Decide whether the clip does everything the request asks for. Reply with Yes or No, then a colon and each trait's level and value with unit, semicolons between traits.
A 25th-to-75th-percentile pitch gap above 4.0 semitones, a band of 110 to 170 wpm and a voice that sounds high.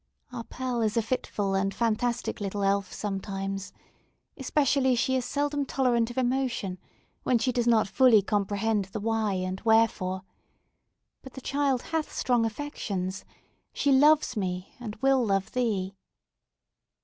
Yes: average, 4.6 semitones; average, 140 wpm; high, 225 Hz